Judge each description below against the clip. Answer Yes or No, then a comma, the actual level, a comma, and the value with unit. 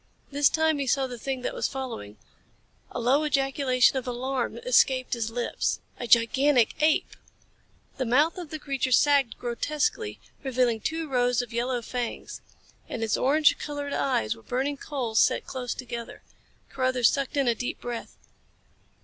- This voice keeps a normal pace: Yes, average, 160 wpm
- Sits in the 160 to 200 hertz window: No, very high, 260 Hz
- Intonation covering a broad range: No, average, 2.9 semitones